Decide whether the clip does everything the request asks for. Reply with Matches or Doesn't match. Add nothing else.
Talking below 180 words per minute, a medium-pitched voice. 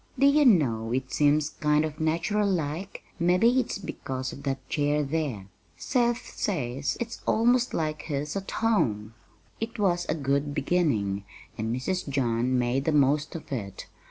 Matches